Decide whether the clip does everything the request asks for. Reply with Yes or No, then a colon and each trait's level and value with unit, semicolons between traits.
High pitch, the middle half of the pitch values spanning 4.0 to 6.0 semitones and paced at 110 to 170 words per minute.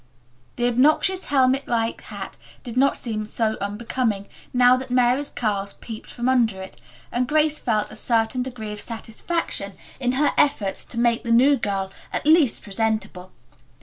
No: high, 240 Hz; average, 3.2 semitones; average, 160 wpm